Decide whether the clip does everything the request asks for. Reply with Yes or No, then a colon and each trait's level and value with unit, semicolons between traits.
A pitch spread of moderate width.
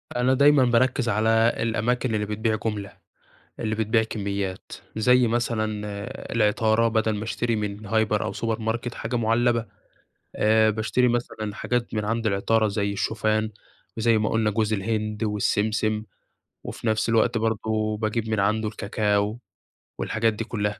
No: narrow, 1.4 semitones